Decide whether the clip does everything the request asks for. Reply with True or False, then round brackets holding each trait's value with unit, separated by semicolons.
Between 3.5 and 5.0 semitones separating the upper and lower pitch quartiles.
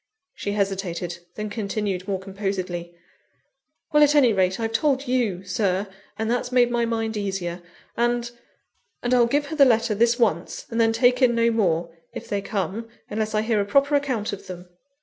True (3.8 semitones)